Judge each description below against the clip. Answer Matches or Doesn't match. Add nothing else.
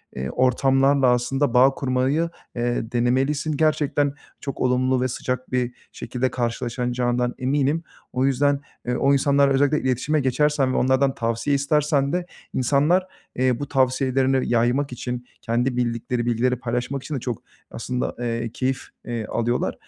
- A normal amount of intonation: Doesn't match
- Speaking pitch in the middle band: Doesn't match